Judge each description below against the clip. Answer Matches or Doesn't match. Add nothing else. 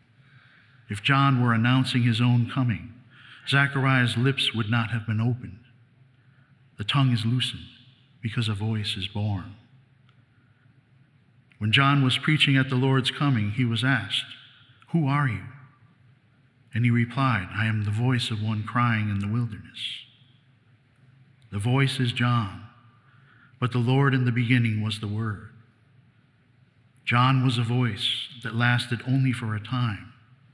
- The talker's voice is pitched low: Matches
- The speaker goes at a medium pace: Matches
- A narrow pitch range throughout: Matches